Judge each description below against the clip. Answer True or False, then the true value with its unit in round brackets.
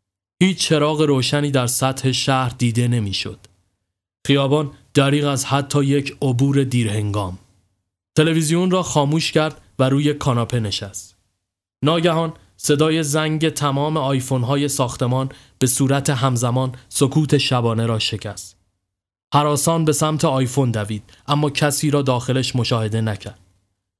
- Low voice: True (130 Hz)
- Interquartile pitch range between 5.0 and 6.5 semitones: True (5.5 semitones)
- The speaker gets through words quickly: False (120 wpm)